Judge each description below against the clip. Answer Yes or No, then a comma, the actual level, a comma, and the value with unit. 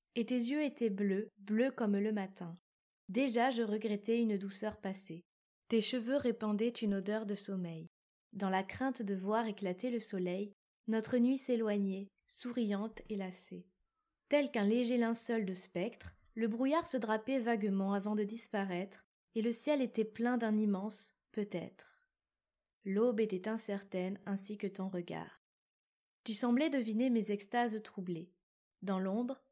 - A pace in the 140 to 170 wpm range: Yes, average, 150 wpm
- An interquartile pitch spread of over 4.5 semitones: No, average, 3.4 semitones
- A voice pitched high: Yes, high, 215 Hz